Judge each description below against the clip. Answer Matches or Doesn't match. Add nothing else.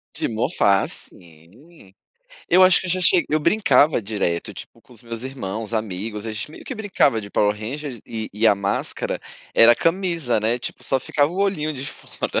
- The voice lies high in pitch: Doesn't match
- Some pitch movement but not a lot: Doesn't match